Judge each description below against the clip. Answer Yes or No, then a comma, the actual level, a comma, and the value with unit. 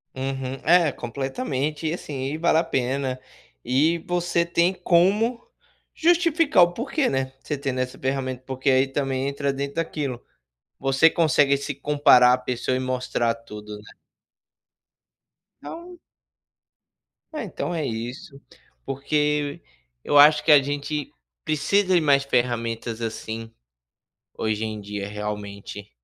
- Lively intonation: No, average, 4.2 semitones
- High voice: No, medium, 140 Hz